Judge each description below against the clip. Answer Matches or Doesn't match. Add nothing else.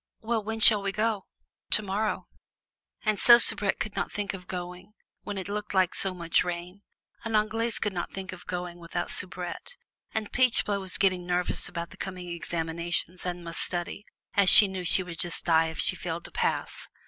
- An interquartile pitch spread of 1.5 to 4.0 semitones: Matches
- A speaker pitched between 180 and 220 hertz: Matches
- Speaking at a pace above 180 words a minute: Matches